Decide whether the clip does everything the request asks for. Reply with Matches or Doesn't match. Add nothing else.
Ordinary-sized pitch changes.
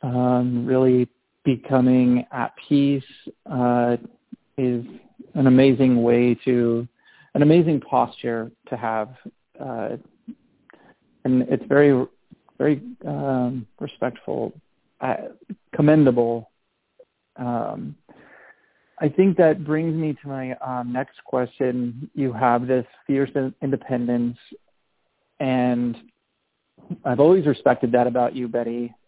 Doesn't match